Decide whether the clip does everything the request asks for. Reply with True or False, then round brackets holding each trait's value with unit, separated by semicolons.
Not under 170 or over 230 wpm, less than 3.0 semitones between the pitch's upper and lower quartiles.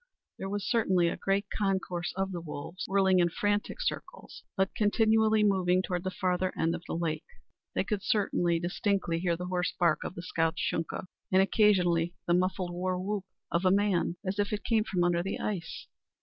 True (190 wpm; 2.6 semitones)